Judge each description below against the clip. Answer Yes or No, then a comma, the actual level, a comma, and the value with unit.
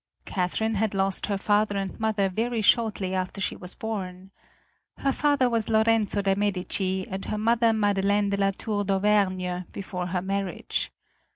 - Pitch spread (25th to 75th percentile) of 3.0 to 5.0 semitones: No, narrow, 2.4 semitones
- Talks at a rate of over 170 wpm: No, average, 160 wpm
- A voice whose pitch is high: Yes, high, 200 Hz